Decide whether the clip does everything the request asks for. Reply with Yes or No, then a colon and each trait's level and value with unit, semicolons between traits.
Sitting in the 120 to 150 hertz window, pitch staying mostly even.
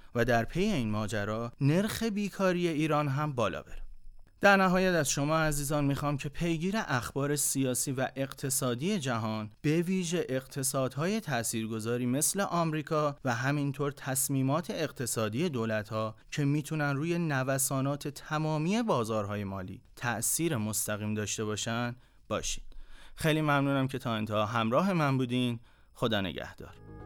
No: low, 135 Hz; average, 5.3 semitones